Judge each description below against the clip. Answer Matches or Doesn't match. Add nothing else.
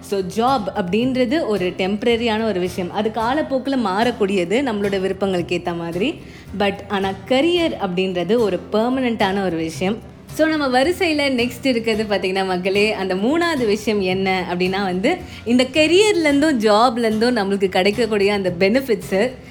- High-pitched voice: Matches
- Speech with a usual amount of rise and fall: Matches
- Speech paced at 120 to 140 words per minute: Matches